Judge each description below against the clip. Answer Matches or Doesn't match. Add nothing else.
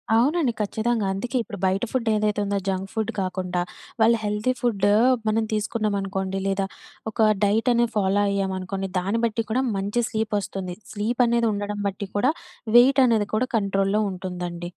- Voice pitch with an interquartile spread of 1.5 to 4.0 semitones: Matches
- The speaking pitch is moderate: Doesn't match